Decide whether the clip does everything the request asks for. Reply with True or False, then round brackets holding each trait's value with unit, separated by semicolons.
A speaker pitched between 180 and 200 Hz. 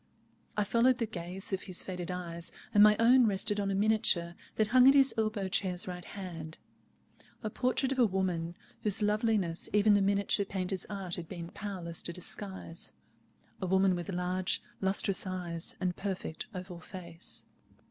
True (190 Hz)